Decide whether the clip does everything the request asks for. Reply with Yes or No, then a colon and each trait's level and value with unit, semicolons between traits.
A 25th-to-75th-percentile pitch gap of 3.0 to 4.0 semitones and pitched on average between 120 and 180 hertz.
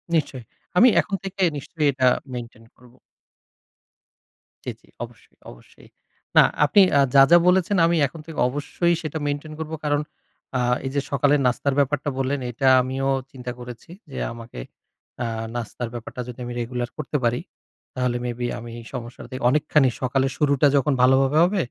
Yes: average, 3.3 semitones; low, 135 Hz